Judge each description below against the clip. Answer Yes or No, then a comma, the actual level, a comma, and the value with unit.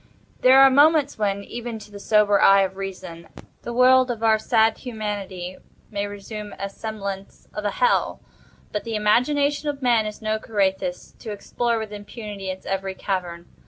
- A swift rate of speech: No, average, 165 wpm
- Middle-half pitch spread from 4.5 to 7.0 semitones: No, average, 3.2 semitones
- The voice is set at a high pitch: Yes, high, 210 Hz